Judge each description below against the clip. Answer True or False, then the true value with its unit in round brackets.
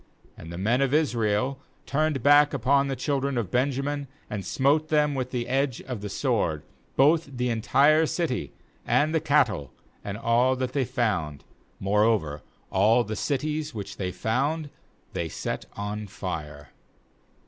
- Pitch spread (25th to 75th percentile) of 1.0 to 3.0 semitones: False (5.4 semitones)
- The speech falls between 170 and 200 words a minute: False (150 wpm)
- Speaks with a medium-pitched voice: False (125 Hz)